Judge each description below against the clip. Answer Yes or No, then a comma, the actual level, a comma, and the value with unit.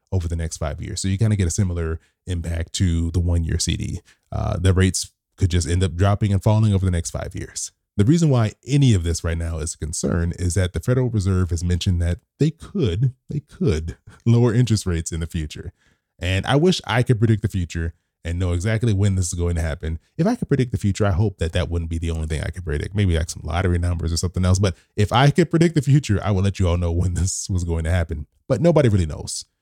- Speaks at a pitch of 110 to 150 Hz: No, very low, 95 Hz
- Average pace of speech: No, fast, 255 wpm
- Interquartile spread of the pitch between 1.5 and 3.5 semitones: No, average, 4.1 semitones